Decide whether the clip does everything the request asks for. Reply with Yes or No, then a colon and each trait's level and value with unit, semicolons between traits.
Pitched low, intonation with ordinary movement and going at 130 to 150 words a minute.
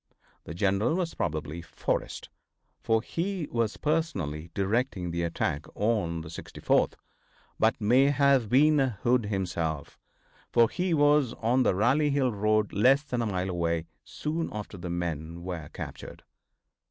No: low, 110 Hz; wide, 8.0 semitones; average, 140 wpm